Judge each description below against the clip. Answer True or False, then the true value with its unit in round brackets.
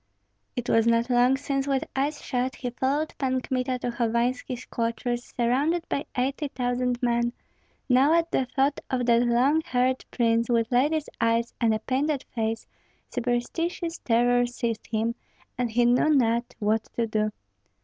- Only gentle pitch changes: True (2.3 semitones)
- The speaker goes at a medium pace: True (160 wpm)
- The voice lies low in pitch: False (245 Hz)